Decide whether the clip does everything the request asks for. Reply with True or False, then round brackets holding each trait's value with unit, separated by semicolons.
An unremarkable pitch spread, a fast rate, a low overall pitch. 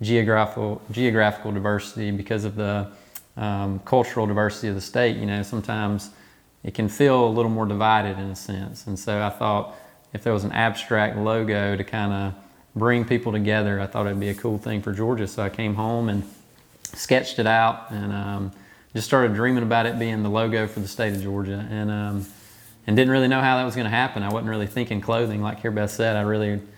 False (1.9 semitones; 215 wpm; 105 Hz)